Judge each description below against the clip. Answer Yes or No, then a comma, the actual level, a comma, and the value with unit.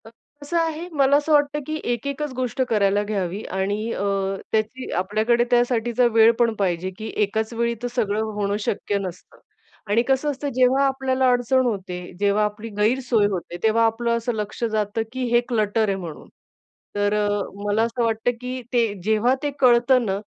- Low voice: No, high, 225 Hz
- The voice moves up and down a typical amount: Yes, average, 3.5 semitones